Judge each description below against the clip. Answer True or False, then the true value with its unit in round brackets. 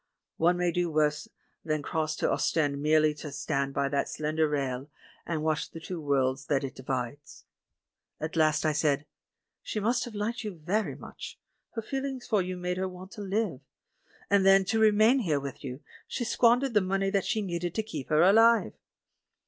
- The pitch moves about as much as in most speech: False (5.7 semitones)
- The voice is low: False (170 Hz)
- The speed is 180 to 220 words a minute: True (195 wpm)